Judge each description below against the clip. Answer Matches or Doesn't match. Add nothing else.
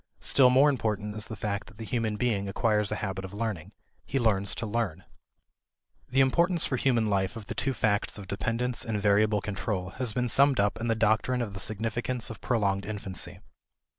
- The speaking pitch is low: Matches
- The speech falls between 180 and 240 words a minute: Matches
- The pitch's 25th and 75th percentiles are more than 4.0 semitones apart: Doesn't match